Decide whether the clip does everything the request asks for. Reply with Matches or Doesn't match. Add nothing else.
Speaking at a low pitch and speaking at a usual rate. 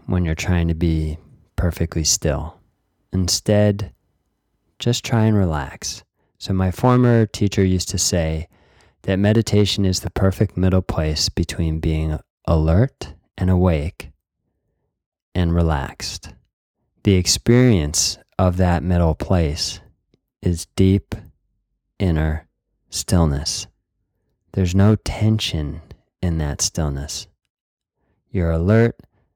Doesn't match